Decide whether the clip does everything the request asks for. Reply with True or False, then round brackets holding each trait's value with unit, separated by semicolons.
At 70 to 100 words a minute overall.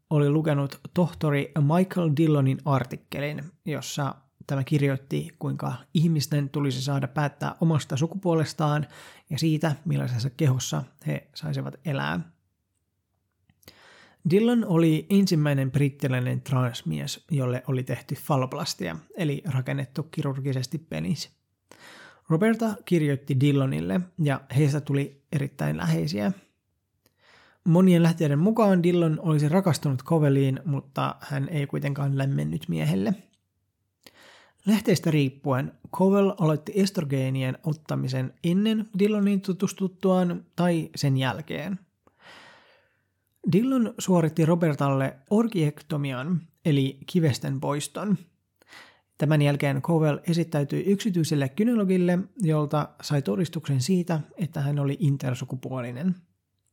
True (95 wpm)